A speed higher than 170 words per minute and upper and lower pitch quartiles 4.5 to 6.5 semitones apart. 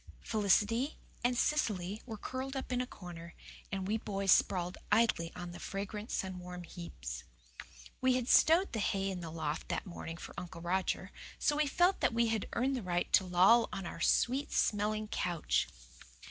Yes: average, 180 wpm; average, 5.1 semitones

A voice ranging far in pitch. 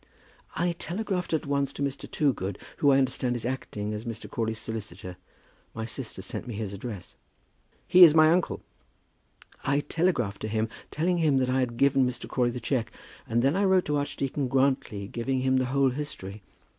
No: average, 4.2 semitones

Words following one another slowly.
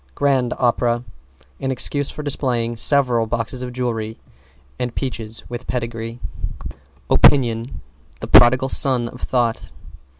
Yes: slow, 120 wpm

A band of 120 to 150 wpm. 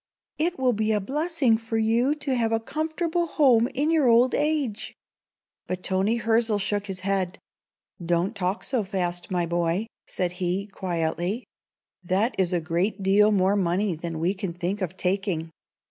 No: average, 165 wpm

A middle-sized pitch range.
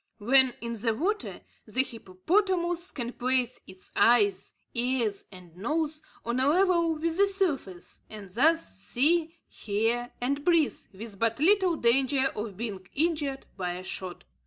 No: wide, 7.1 semitones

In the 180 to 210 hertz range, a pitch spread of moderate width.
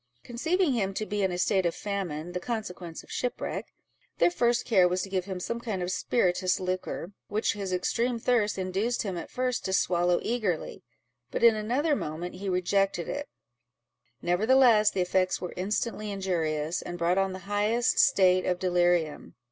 Yes: high, 190 Hz; average, 3.9 semitones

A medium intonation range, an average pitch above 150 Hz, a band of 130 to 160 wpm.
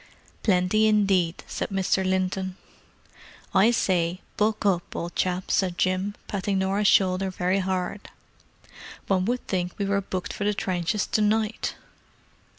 No: narrow, 1.9 semitones; high, 190 Hz; average, 140 wpm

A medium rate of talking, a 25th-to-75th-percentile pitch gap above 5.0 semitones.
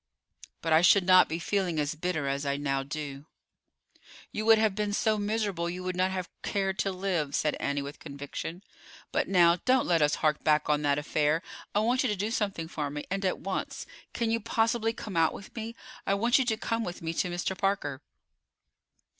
No: fast, 210 wpm; wide, 5.4 semitones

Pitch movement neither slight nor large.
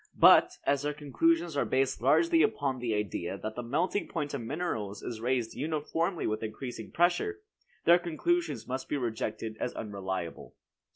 No: wide, 6.9 semitones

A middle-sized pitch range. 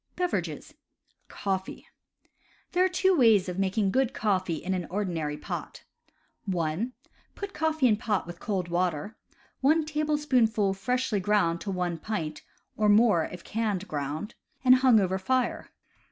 No: wide, 5.9 semitones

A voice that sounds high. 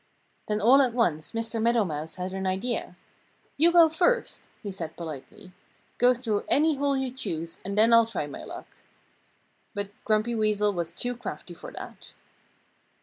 Yes: high, 220 Hz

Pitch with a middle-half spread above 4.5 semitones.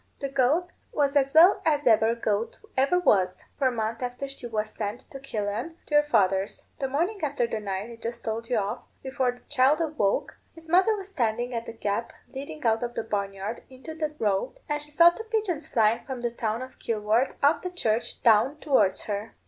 Yes: average, 5.2 semitones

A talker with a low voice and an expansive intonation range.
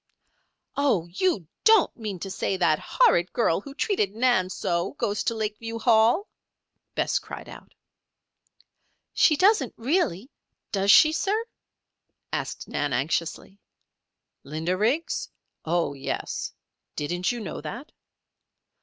No: high, 210 Hz; wide, 7.9 semitones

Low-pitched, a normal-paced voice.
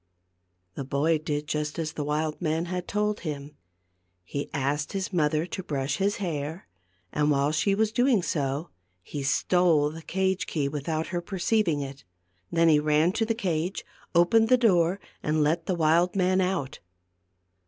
No: medium, 160 Hz; average, 165 wpm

